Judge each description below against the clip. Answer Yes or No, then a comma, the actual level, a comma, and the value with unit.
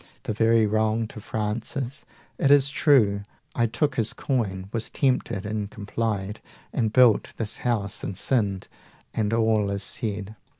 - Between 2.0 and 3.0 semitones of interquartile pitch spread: Yes, narrow, 2.4 semitones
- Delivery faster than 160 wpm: No, average, 145 wpm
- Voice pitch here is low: Yes, low, 110 Hz